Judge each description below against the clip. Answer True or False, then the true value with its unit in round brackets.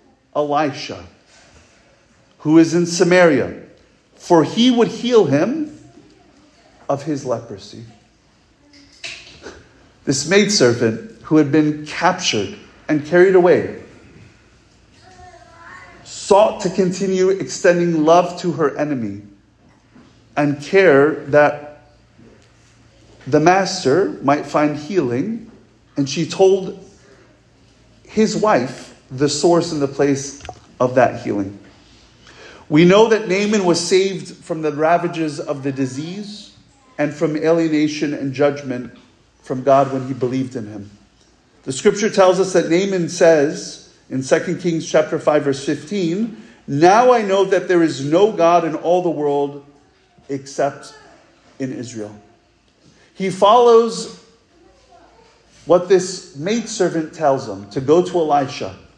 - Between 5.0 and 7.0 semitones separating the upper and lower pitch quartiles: True (5.4 semitones)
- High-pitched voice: False (155 Hz)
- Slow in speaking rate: True (115 wpm)